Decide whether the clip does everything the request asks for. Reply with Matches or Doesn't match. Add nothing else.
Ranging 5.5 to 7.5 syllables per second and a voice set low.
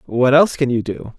Matches